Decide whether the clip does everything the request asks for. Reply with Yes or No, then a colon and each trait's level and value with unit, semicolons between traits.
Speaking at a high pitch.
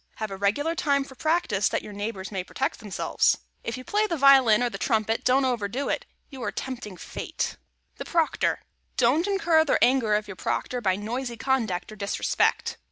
Yes: high, 245 Hz